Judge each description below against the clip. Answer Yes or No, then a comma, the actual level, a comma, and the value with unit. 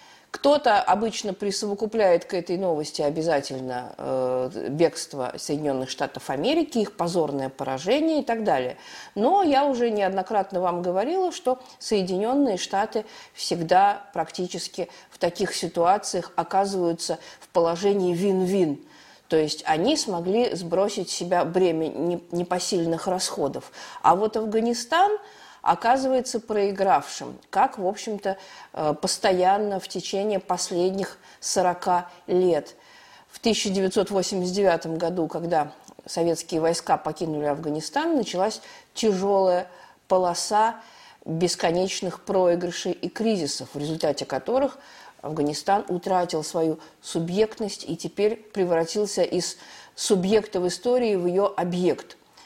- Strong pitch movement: No, average, 3.8 semitones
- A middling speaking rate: No, slow, 105 wpm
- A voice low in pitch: No, medium, 185 Hz